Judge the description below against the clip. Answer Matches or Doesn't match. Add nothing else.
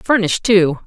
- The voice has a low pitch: Doesn't match